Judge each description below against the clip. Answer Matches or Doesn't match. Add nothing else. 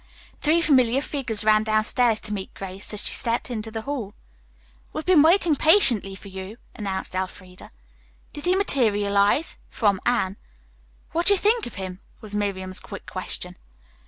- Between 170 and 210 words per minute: Doesn't match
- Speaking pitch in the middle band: Doesn't match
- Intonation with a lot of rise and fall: Matches